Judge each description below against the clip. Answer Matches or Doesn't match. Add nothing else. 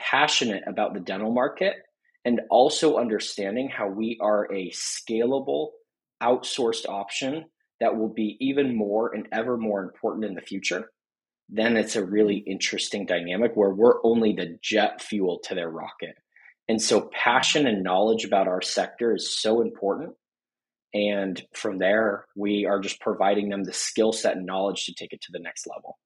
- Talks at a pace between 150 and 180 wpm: Matches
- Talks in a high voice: Doesn't match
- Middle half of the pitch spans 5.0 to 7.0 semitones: Doesn't match